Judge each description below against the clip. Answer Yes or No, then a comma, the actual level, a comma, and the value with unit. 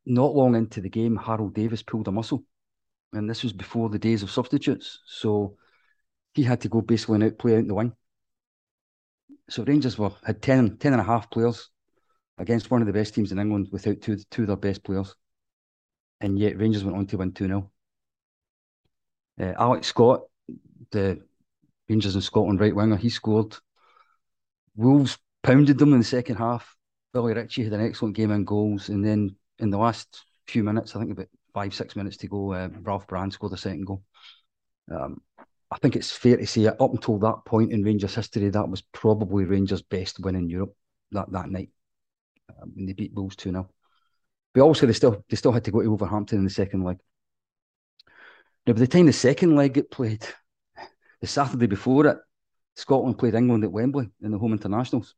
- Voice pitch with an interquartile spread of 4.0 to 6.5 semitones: No, average, 3.2 semitones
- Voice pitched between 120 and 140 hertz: No, low, 110 Hz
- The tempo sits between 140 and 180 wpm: No, average, 195 wpm